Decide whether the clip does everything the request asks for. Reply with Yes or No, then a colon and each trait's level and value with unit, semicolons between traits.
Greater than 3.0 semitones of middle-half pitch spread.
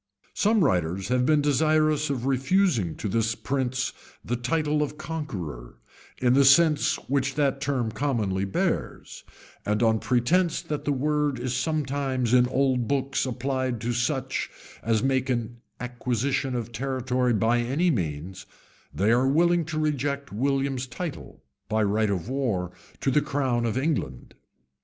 Yes: average, 3.4 semitones